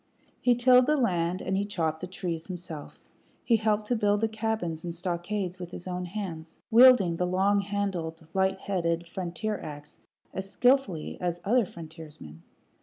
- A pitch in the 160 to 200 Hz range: Yes, medium, 185 Hz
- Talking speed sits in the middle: Yes, average, 160 wpm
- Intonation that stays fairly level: No, average, 3.8 semitones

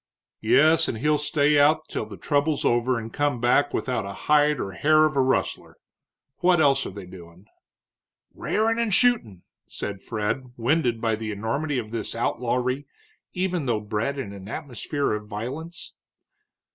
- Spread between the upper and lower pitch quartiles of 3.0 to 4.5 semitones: No, wide, 5.5 semitones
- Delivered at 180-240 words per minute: No, average, 160 wpm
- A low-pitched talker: Yes, low, 130 Hz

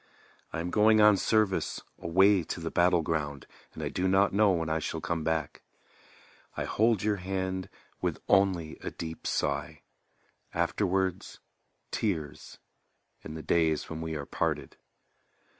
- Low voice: Yes, very low, 90 Hz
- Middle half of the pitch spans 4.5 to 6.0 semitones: No, average, 3.4 semitones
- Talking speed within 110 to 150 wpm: Yes, average, 145 wpm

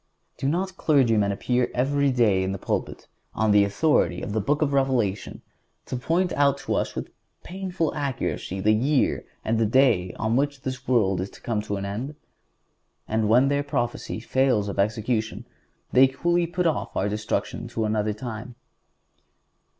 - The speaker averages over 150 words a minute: Yes, average, 170 wpm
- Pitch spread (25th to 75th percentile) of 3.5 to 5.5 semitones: Yes, average, 5.0 semitones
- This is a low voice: Yes, low, 120 Hz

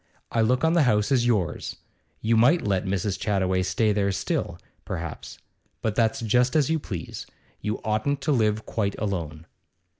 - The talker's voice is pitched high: No, low, 110 Hz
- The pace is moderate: Yes, average, 170 wpm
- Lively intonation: No, average, 3.8 semitones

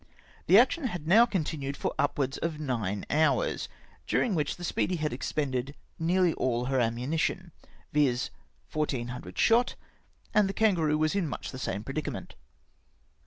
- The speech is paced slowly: No, average, 150 wpm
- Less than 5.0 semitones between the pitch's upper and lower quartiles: No, wide, 5.4 semitones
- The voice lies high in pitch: No, medium, 150 Hz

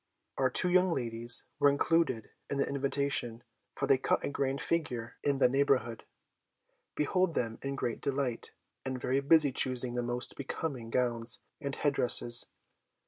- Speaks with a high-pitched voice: No, low, 135 Hz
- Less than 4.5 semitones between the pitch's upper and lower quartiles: Yes, average, 2.8 semitones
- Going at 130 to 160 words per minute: Yes, average, 155 wpm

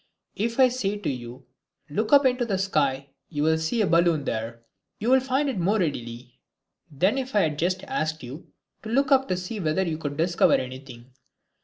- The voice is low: No, medium, 170 Hz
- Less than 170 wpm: No, average, 200 wpm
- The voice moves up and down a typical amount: No, wide, 8.2 semitones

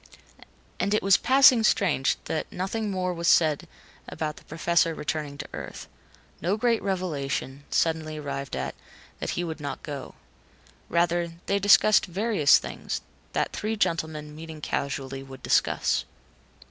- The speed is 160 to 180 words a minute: No, average, 140 wpm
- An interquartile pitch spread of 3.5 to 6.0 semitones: Yes, average, 4.7 semitones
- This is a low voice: No, medium, 165 Hz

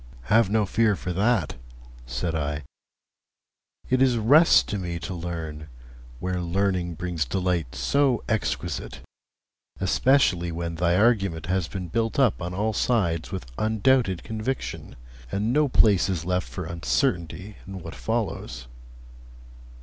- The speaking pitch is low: Yes, very low, 90 Hz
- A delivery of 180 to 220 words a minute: No, slow, 135 wpm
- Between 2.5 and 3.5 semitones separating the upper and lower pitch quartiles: No, average, 4.7 semitones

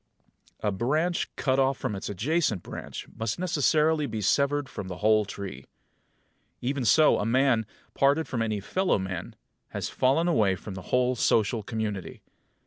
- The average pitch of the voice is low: Yes, low, 120 Hz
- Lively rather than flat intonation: Yes, wide, 5.7 semitones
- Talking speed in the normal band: Yes, average, 155 wpm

